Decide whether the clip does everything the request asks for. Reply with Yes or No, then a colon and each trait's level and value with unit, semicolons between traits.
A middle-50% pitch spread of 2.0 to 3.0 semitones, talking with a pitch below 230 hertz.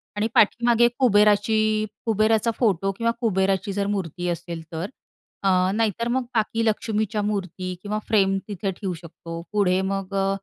Yes: narrow, 2.6 semitones; high, 200 Hz